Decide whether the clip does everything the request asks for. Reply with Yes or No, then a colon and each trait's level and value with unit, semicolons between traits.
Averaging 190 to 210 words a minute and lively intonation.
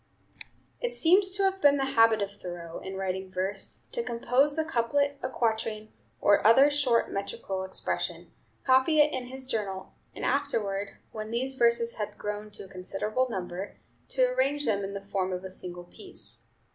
No: average, 175 wpm; wide, 6.1 semitones